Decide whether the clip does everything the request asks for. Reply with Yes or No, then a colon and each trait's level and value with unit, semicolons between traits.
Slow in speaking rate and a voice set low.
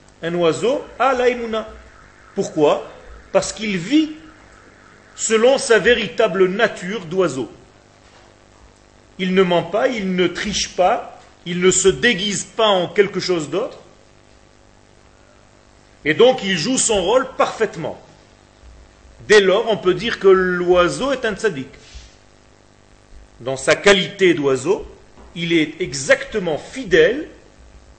No: slow, 120 wpm; medium, 185 Hz